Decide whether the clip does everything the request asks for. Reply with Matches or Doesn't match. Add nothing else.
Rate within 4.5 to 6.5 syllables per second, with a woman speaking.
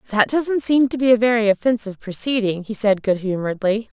Matches